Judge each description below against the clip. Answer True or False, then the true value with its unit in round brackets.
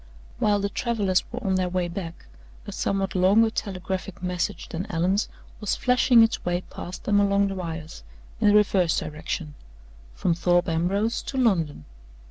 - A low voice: False (190 Hz)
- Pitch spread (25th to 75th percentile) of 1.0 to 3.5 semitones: True (2.8 semitones)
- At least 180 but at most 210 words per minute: False (160 wpm)